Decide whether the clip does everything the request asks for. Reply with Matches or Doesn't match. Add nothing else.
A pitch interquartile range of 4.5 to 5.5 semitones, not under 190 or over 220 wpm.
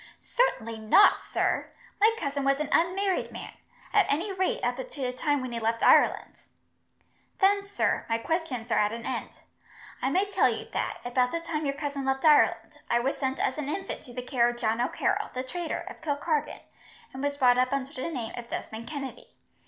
Matches